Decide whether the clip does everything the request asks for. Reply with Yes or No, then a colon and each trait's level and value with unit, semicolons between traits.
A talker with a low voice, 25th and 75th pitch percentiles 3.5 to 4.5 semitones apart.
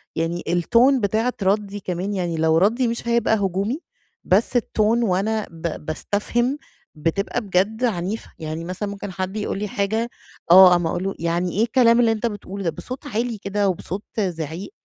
No: high, 200 Hz; average, 4.0 semitones